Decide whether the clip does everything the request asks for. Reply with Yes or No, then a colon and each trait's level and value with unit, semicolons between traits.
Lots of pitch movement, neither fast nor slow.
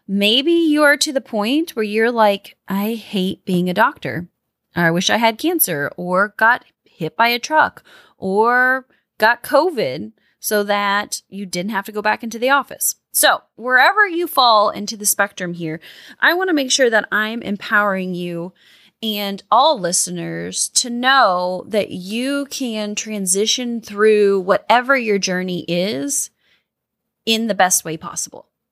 No: average, 4.4 semitones; average, 160 wpm